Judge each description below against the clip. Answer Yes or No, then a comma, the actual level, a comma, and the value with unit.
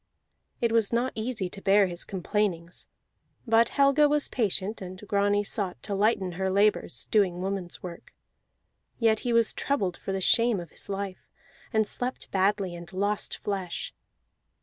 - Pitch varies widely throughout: No, average, 3.2 semitones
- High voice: Yes, high, 200 Hz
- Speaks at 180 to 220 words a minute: No, average, 155 wpm